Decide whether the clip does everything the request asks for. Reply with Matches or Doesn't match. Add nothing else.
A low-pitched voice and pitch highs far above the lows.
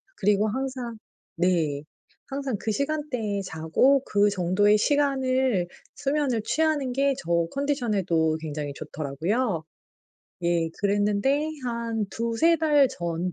Doesn't match